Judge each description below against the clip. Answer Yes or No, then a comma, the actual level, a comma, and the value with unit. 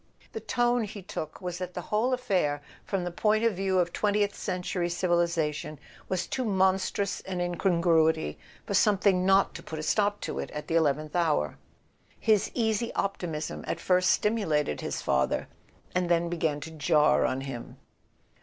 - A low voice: No, medium, 180 Hz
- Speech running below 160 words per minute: No, average, 170 wpm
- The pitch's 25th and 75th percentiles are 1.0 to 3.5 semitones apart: No, average, 4.0 semitones